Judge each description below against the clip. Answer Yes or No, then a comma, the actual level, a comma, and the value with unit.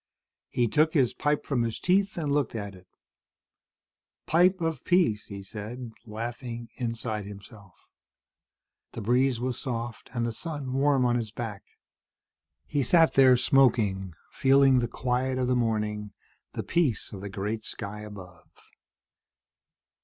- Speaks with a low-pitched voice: Yes, low, 120 Hz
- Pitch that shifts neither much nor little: Yes, average, 4.2 semitones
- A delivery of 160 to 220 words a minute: No, average, 140 wpm